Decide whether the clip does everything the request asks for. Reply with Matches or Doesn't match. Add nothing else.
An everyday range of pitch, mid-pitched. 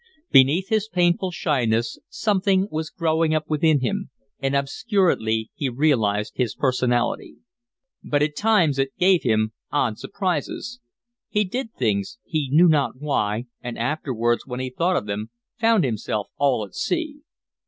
Doesn't match